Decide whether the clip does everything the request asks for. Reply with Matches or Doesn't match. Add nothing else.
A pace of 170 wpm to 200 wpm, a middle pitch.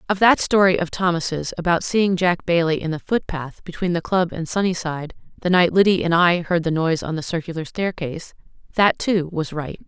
Matches